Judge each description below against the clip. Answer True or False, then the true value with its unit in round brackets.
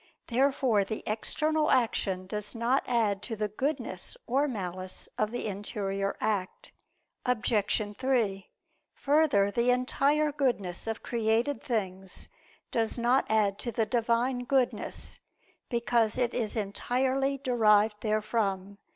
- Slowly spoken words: True (120 wpm)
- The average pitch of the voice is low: False (225 Hz)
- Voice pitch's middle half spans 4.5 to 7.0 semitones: False (3.7 semitones)